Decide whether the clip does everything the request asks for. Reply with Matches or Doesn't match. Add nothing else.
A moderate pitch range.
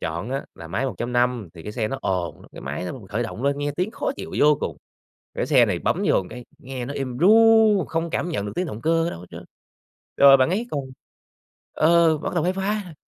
Doesn't match